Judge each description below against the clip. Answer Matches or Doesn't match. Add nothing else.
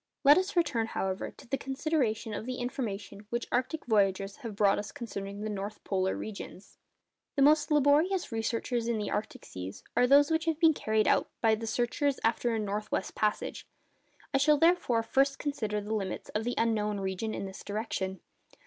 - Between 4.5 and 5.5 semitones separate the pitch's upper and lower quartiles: Matches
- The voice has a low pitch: Doesn't match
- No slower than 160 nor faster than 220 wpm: Matches